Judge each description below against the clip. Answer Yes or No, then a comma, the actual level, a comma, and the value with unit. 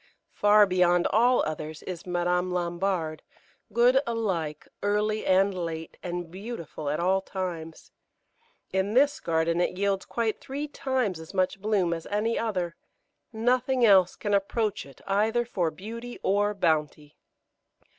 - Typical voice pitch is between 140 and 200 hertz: Yes, high, 190 Hz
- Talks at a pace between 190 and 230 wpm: No, slow, 135 wpm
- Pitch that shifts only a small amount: No, average, 4.1 semitones